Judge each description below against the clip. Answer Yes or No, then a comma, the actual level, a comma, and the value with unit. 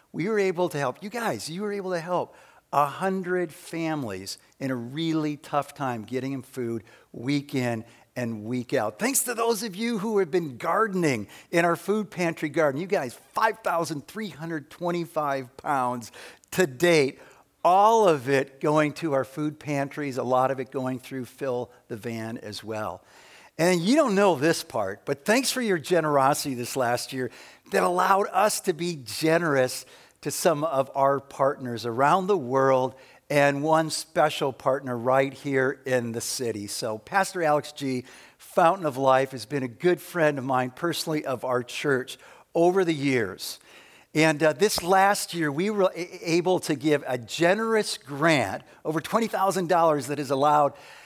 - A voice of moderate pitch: Yes, medium, 150 Hz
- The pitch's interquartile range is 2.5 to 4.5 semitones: No, average, 5.2 semitones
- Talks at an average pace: Yes, average, 165 wpm